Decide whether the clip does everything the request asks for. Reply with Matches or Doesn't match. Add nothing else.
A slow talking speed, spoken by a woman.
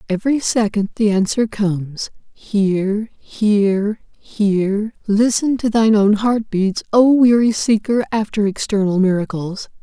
Matches